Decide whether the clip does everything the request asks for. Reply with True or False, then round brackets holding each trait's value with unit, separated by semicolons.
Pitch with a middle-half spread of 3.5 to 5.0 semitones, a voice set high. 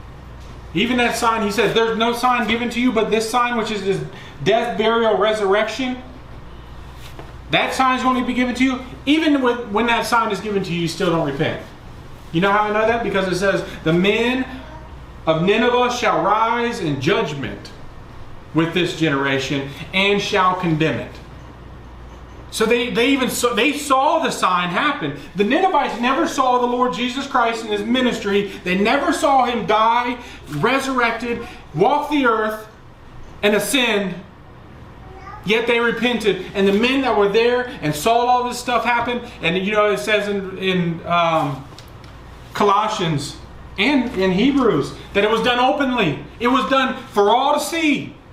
True (4.4 semitones; 225 Hz)